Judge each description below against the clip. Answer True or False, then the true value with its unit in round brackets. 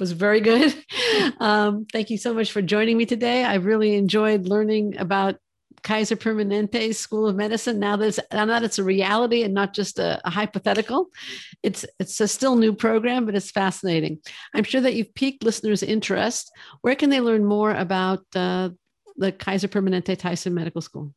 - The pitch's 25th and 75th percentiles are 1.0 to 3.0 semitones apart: True (2.6 semitones)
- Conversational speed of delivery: True (185 wpm)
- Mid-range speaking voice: False (215 Hz)